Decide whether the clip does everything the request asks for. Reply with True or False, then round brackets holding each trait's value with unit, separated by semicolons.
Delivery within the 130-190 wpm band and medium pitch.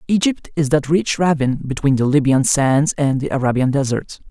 True (180 wpm; 145 Hz)